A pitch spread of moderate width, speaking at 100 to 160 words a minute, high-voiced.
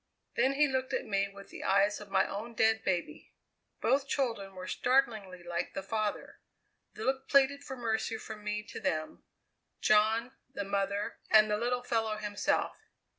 No: average, 3.7 semitones; average, 170 wpm; high, 215 Hz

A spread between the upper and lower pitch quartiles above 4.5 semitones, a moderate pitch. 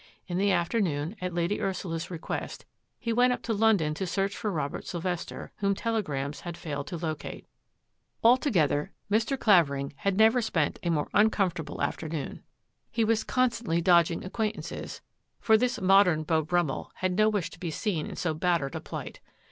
Yes: average, 4.9 semitones; medium, 180 Hz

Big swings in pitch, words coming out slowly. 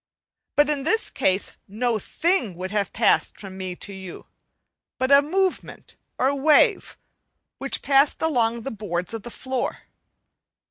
No: wide, 6.4 semitones; average, 145 wpm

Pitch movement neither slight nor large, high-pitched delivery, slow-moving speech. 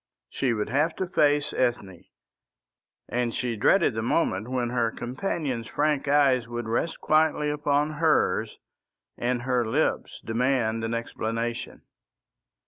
No: average, 4.1 semitones; low, 125 Hz; slow, 130 wpm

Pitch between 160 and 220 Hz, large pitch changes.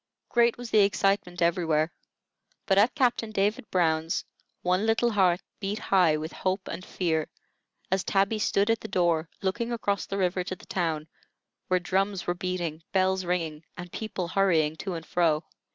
No: medium, 185 Hz; average, 2.9 semitones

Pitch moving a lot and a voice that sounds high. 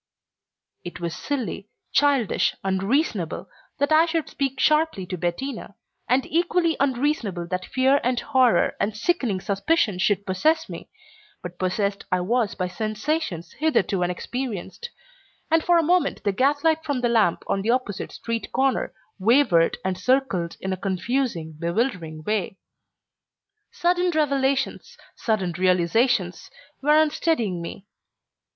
Yes: wide, 7.3 semitones; high, 235 Hz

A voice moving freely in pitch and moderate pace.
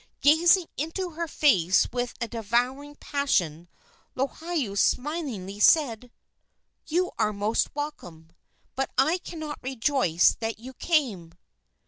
No: wide, 6.5 semitones; slow, 110 wpm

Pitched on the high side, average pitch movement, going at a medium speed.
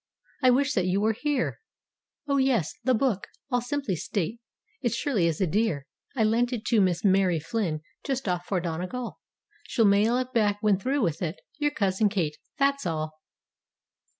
No: high, 210 Hz; wide, 5.8 semitones; average, 175 wpm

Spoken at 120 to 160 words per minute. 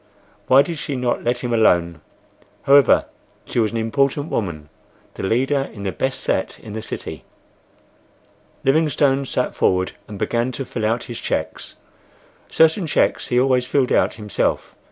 Yes: average, 155 wpm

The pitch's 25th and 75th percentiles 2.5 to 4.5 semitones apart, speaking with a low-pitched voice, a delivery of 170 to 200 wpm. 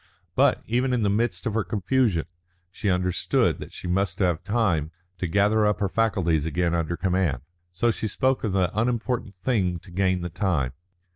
Yes: average, 3.9 semitones; very low, 95 Hz; average, 185 wpm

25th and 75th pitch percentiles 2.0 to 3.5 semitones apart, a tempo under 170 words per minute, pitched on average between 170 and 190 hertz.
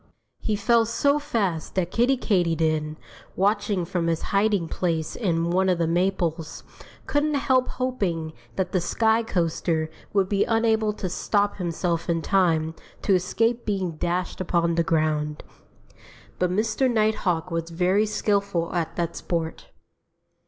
No: average, 4.3 semitones; average, 140 wpm; medium, 185 Hz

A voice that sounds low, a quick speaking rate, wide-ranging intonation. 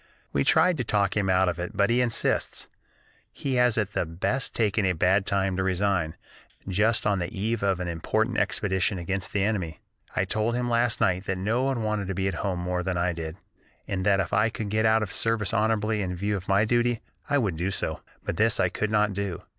No: low, 100 Hz; fast, 235 wpm; average, 3.0 semitones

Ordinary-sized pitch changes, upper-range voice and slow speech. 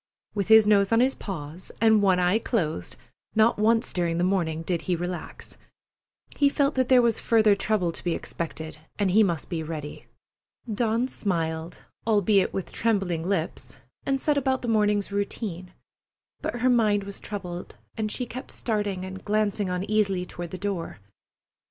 No: average, 3.8 semitones; high, 200 Hz; average, 165 wpm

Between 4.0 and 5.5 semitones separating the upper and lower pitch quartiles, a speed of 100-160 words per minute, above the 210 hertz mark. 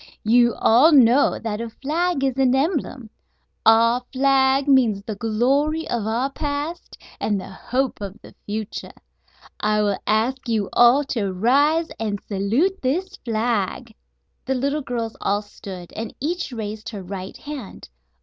Yes: average, 4.4 semitones; average, 150 wpm; high, 240 Hz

